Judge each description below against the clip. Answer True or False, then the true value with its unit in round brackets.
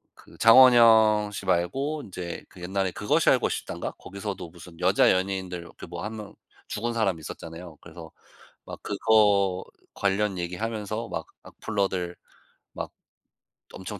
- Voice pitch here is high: False (95 Hz)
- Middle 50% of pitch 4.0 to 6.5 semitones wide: False (3.3 semitones)